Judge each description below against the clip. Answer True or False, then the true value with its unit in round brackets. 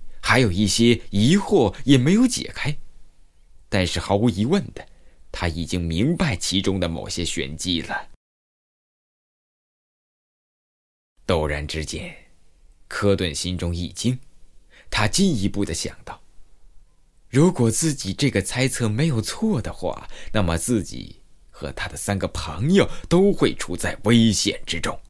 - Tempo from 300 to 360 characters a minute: False (190 characters per minute)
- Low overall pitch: True (100 Hz)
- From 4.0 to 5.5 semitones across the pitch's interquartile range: False (7.2 semitones)